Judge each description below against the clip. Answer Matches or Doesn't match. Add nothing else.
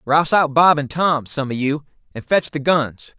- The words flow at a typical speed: Doesn't match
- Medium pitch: Matches